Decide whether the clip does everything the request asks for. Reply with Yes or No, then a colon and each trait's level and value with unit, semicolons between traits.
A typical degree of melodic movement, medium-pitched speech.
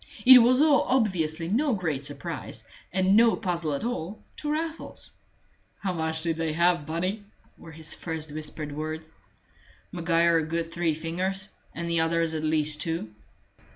Yes: average, 3.3 semitones; medium, 165 Hz